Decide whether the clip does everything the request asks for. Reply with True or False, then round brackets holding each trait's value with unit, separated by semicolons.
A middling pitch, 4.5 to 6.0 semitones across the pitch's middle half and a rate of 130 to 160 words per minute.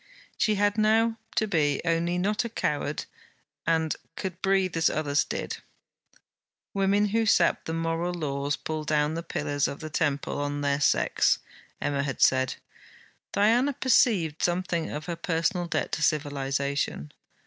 True (165 Hz; 5.0 semitones; 150 wpm)